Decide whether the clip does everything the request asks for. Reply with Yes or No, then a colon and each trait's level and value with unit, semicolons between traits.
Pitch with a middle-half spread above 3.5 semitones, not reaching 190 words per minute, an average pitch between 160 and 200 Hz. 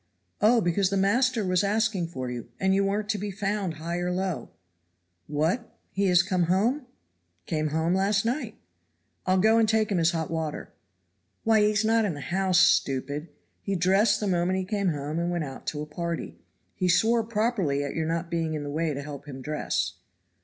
No: average, 4.5 semitones; fast, 205 wpm; medium, 185 Hz